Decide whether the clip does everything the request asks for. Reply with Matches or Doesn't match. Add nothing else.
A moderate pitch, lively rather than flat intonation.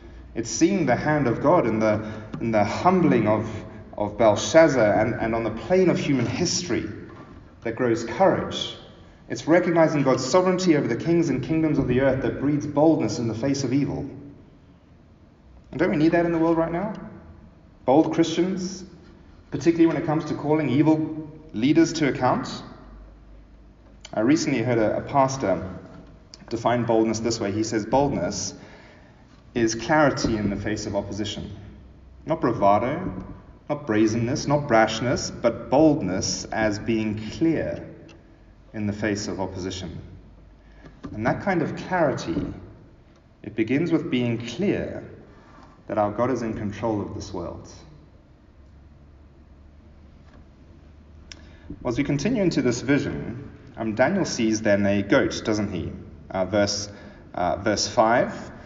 Doesn't match